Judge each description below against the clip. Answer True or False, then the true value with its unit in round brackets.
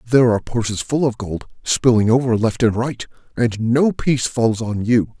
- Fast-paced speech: False (195 wpm)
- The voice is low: True (115 Hz)